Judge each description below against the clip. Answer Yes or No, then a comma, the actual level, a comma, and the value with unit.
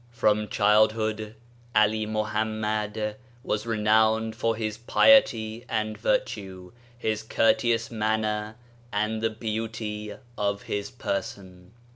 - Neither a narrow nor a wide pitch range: No, narrow, 0.8 semitones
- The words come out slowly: Yes, slow, 100 wpm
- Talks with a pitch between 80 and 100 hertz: No, low, 110 Hz